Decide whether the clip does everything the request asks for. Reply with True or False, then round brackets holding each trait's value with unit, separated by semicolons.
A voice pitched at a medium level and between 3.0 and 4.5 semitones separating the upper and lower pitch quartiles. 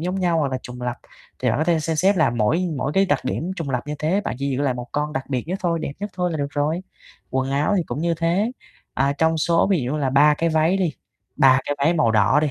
True (150 Hz; 4.0 semitones)